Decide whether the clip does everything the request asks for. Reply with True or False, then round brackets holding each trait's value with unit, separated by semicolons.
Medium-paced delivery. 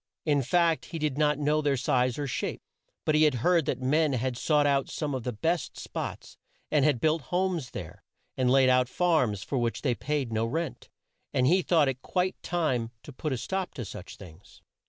False (210 wpm)